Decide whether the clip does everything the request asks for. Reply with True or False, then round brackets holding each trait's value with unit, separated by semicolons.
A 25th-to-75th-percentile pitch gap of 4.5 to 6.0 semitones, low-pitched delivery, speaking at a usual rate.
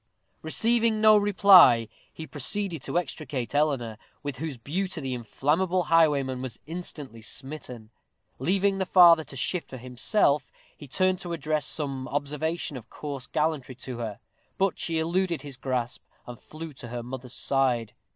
False (5.2 semitones; 150 Hz; 150 wpm)